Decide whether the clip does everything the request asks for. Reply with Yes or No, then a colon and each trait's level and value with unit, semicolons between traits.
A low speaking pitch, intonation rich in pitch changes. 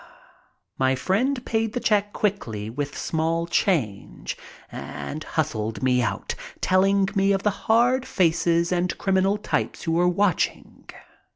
No: medium, 180 Hz; wide, 5.7 semitones